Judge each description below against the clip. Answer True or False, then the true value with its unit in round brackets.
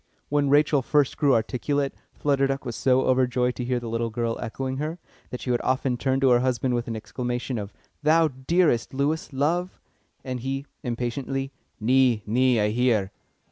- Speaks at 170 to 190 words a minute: True (180 wpm)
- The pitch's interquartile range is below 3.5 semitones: True (2.4 semitones)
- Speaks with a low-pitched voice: True (130 Hz)